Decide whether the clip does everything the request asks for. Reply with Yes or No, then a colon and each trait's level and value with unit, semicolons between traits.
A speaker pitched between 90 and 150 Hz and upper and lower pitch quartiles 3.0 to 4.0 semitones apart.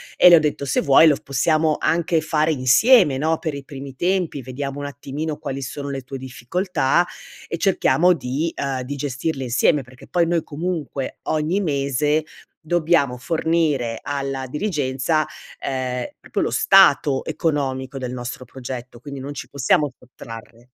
Yes: medium, 140 Hz; average, 3.3 semitones